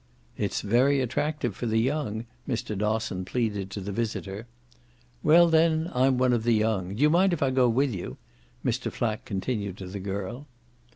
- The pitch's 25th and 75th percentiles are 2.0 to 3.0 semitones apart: No, average, 4.9 semitones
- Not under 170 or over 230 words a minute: Yes, average, 180 wpm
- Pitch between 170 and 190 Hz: No, low, 115 Hz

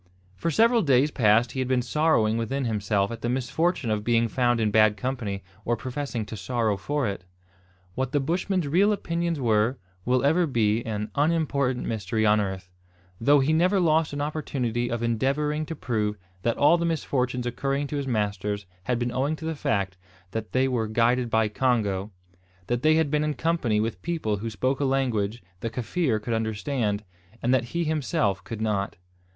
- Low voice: Yes, low, 120 Hz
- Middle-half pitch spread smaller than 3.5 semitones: No, average, 5.0 semitones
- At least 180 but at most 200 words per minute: Yes, average, 185 wpm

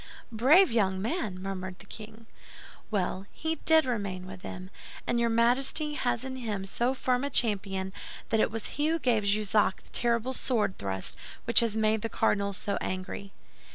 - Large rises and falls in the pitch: No, average, 4.2 semitones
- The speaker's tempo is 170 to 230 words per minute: Yes, average, 175 wpm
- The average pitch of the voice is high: Yes, high, 220 Hz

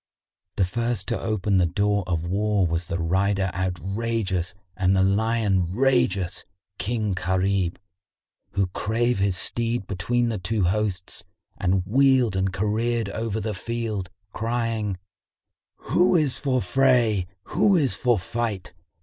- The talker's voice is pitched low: Yes, low, 105 Hz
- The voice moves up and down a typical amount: Yes, average, 3.8 semitones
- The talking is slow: Yes, slow, 130 wpm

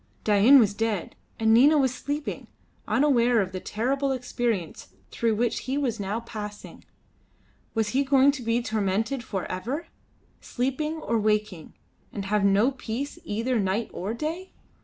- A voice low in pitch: No, high, 230 Hz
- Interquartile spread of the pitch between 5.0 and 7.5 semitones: No, average, 4.3 semitones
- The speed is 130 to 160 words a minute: Yes, average, 150 wpm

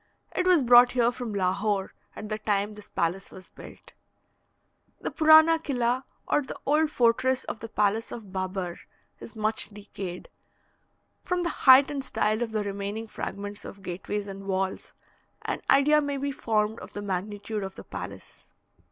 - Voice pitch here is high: Yes, high, 215 Hz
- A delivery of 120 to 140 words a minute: No, average, 165 wpm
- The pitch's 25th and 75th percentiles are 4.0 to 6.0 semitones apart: Yes, average, 4.6 semitones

